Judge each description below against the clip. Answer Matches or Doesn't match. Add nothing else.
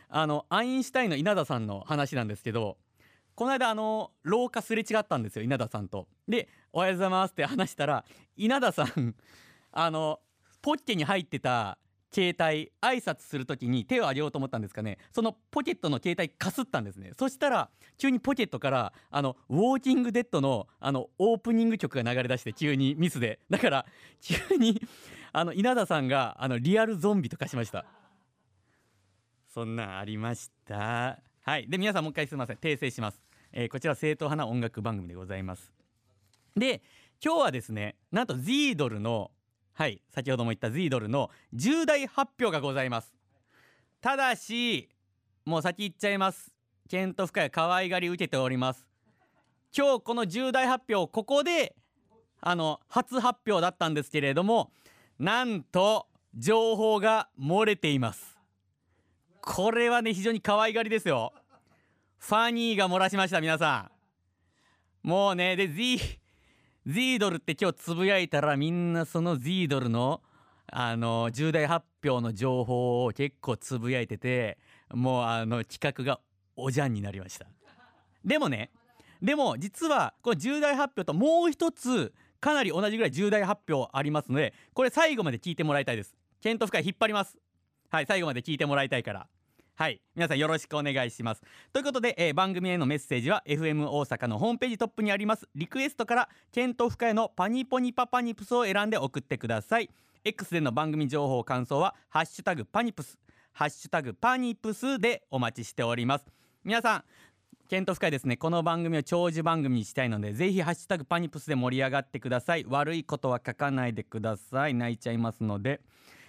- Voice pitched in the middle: Matches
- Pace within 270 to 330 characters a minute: Doesn't match